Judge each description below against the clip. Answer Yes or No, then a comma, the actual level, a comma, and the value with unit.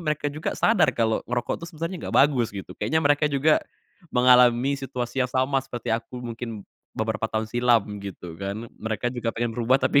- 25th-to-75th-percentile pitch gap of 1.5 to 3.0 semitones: No, average, 3.7 semitones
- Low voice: Yes, low, 120 Hz